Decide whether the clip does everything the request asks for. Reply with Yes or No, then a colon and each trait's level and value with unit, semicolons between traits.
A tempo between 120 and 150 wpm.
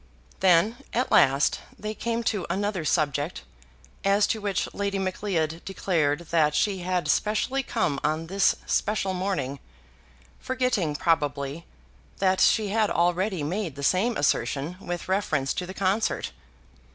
Yes: slow, 135 wpm